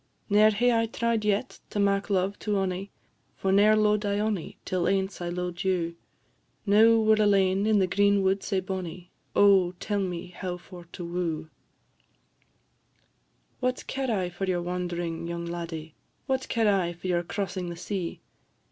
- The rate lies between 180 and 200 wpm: No, average, 170 wpm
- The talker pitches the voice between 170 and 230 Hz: Yes, high, 190 Hz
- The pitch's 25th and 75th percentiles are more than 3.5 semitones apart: No, average, 2.9 semitones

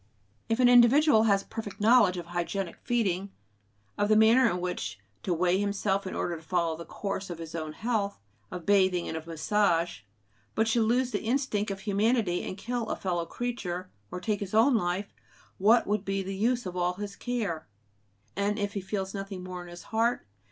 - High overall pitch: Yes, high, 200 Hz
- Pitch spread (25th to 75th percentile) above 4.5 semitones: No, average, 3.7 semitones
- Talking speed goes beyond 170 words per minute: Yes, average, 200 wpm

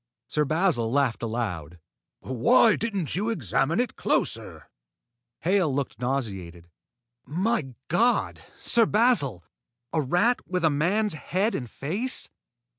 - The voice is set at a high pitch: No, medium, 155 Hz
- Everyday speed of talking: No, slow, 115 wpm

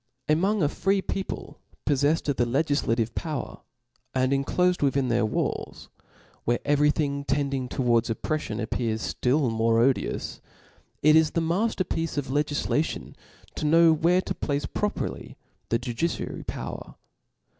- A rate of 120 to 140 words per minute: Yes, slow, 135 wpm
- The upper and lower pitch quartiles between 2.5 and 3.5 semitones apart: No, average, 4.1 semitones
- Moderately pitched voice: Yes, medium, 145 Hz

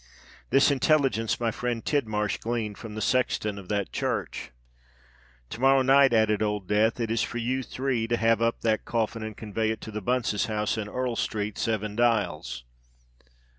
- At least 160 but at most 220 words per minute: Yes, average, 175 wpm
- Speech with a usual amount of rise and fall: No, narrow, 2.2 semitones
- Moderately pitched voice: No, low, 115 Hz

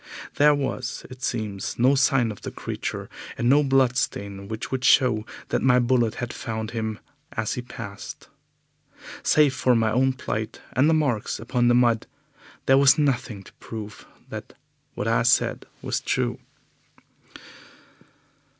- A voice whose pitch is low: Yes, low, 120 Hz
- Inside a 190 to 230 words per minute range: No, average, 150 wpm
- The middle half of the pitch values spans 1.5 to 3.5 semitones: Yes, average, 3.2 semitones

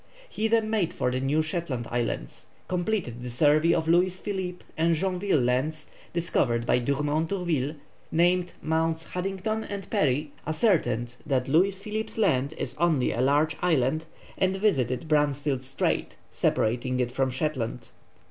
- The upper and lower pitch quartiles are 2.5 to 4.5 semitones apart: No, wide, 5.6 semitones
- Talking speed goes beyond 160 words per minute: No, average, 145 wpm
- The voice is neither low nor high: Yes, medium, 155 Hz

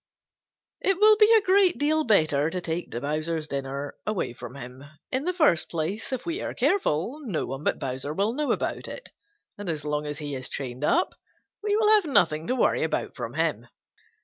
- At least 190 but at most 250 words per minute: Yes, average, 200 wpm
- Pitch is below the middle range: No, medium, 170 Hz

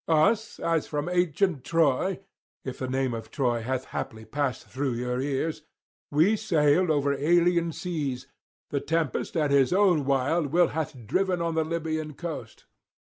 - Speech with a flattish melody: No, average, 4.0 semitones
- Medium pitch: Yes, medium, 155 Hz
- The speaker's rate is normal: Yes, average, 155 wpm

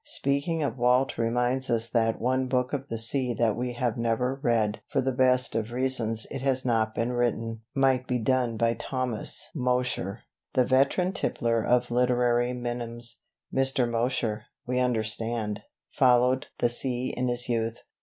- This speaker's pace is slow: No, average, 160 wpm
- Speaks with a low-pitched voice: Yes, low, 125 Hz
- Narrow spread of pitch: Yes, narrow, 1.8 semitones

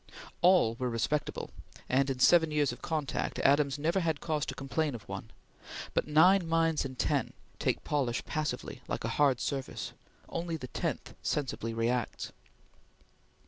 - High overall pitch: No, medium, 145 Hz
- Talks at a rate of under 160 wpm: Yes, average, 150 wpm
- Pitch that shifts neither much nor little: Yes, average, 3.9 semitones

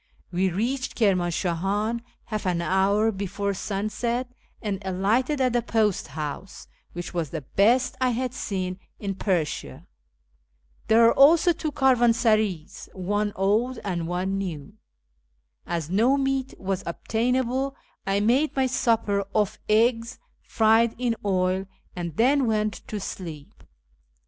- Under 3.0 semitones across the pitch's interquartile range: No, average, 4.3 semitones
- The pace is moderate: No, slow, 130 wpm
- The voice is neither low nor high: No, high, 210 Hz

